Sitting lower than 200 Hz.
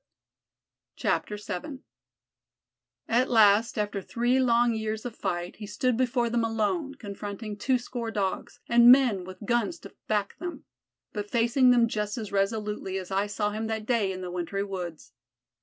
No: high, 220 Hz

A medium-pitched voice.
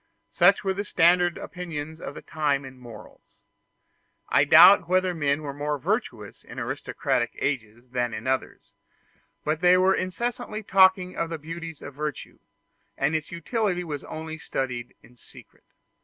Yes: medium, 160 Hz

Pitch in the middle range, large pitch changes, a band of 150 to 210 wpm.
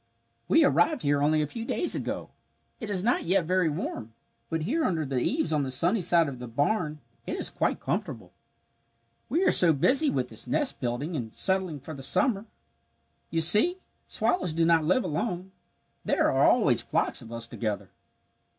Yes: medium, 165 Hz; wide, 6.0 semitones; average, 185 wpm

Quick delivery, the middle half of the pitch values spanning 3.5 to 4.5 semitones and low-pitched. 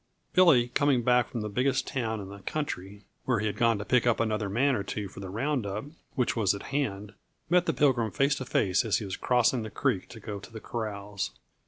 Yes: fast, 240 wpm; average, 3.9 semitones; low, 115 Hz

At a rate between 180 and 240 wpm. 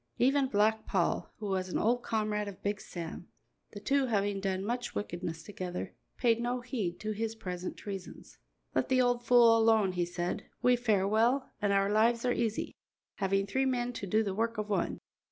Yes: average, 190 wpm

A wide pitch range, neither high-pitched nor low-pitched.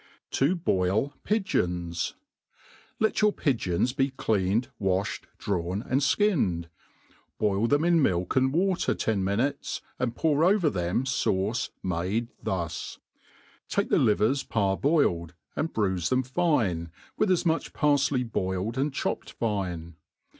No: wide, 7.5 semitones; low, 115 Hz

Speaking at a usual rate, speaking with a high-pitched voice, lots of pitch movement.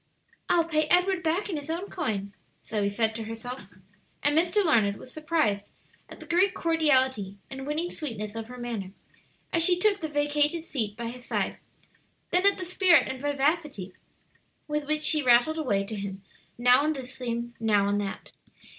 Yes: average, 180 wpm; very high, 275 Hz; wide, 6.5 semitones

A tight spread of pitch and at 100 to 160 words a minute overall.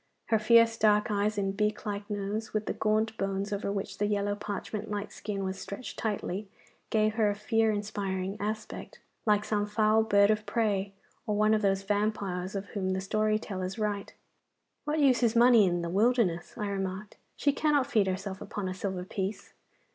No: narrow, 1.7 semitones; average, 185 wpm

